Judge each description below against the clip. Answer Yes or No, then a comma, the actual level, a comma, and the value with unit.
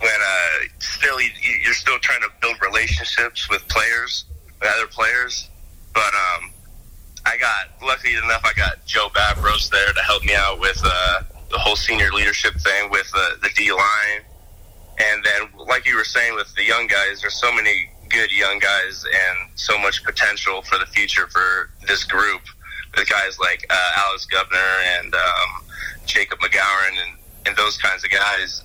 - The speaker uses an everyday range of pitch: Yes, average, 4.8 semitones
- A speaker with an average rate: Yes, average, 175 wpm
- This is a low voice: Yes, very low, 85 Hz